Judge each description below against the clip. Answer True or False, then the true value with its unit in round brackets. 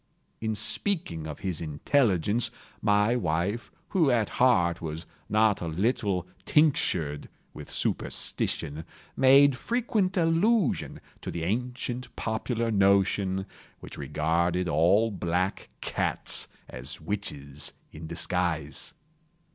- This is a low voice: True (100 Hz)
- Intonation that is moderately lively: False (6.5 semitones)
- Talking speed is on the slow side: True (105 wpm)